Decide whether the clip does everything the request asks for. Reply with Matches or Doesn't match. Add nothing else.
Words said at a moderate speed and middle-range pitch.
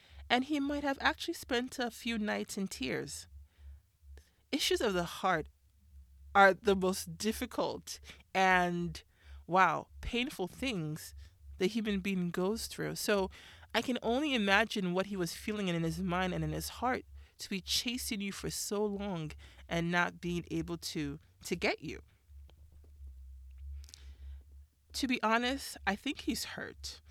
Matches